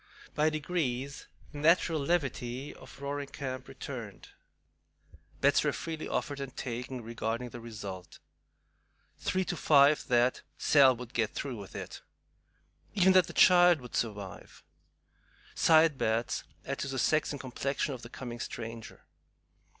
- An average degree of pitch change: Yes, average, 4.1 semitones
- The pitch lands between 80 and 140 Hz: Yes, low, 135 Hz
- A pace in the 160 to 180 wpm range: No, average, 140 wpm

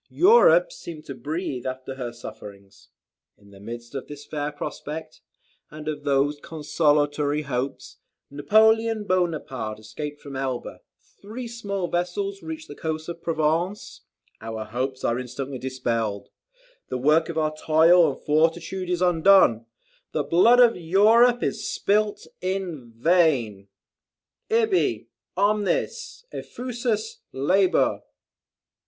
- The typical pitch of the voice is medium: Yes, medium, 155 Hz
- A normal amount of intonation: No, wide, 7.0 semitones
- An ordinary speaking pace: No, slow, 120 wpm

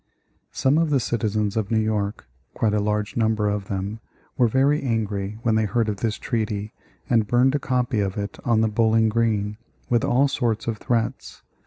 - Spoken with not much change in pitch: Yes, narrow, 2.2 semitones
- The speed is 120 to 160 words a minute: No, average, 190 wpm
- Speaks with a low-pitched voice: Yes, low, 110 Hz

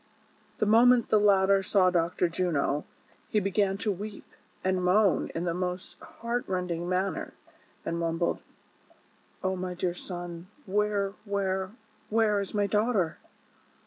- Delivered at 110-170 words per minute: Yes, average, 155 wpm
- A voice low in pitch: No, high, 190 Hz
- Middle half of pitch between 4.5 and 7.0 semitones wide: No, narrow, 2.6 semitones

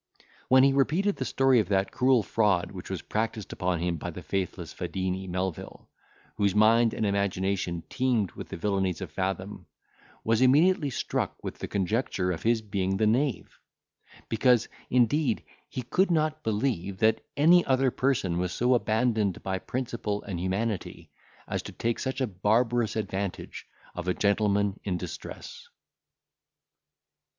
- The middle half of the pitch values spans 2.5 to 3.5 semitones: No, average, 4.9 semitones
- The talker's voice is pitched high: No, low, 105 Hz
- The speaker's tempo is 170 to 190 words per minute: No, average, 150 wpm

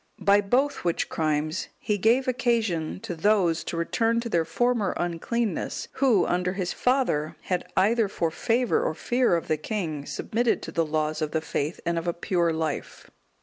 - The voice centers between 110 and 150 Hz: No, medium, 180 Hz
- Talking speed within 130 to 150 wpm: No, average, 185 wpm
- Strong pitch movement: Yes, wide, 6.1 semitones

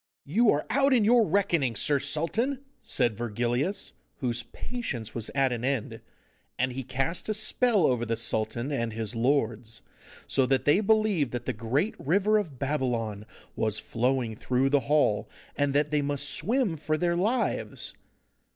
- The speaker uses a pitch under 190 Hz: Yes, medium, 140 Hz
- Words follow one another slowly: No, average, 160 wpm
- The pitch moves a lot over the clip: Yes, wide, 7.3 semitones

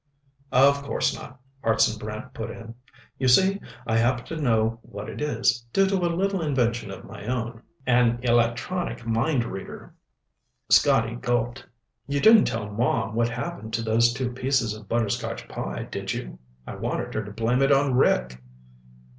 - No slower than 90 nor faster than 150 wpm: No, average, 165 wpm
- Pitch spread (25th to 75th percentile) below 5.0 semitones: Yes, average, 3.3 semitones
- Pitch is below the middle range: Yes, low, 120 Hz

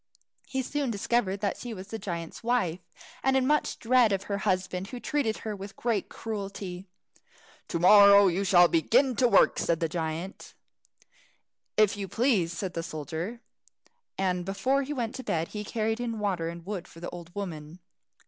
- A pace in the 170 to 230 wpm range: Yes, average, 175 wpm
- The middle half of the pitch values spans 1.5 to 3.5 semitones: No, average, 4.7 semitones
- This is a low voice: No, high, 200 Hz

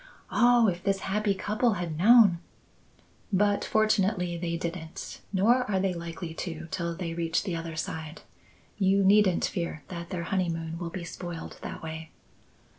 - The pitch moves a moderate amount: Yes, average, 3.0 semitones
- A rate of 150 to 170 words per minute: Yes, average, 160 wpm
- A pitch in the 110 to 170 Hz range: No, medium, 180 Hz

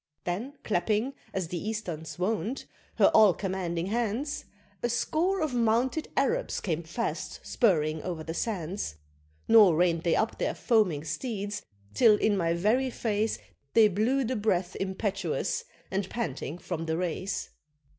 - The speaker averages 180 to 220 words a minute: No, average, 145 wpm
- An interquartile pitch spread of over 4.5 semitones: Yes, average, 4.9 semitones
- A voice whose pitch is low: No, high, 200 Hz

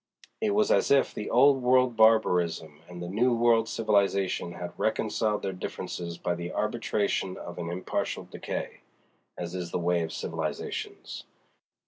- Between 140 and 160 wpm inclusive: Yes, average, 145 wpm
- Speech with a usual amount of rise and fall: Yes, average, 4.9 semitones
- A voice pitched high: No, low, 100 Hz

